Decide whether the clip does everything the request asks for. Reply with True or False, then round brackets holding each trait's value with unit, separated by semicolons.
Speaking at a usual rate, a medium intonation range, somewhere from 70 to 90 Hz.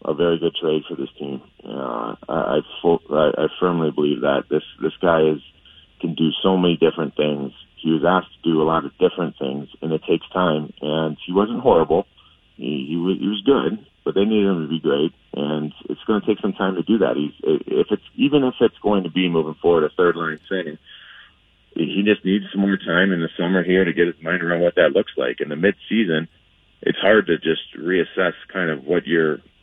False (230 wpm; 3.6 semitones; 85 Hz)